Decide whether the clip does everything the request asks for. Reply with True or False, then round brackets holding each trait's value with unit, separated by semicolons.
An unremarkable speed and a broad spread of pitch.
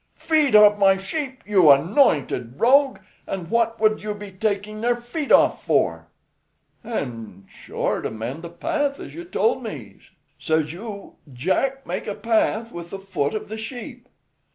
True (160 wpm; 6.0 semitones)